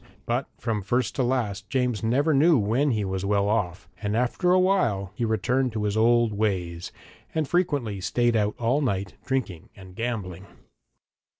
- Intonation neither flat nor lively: Yes, average, 4.4 semitones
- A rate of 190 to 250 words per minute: No, average, 170 wpm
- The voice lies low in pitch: Yes, low, 110 Hz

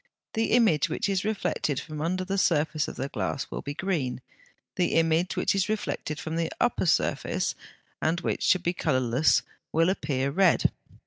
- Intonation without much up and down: No, average, 4.0 semitones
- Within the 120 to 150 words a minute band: No, average, 175 wpm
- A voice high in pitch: No, medium, 165 Hz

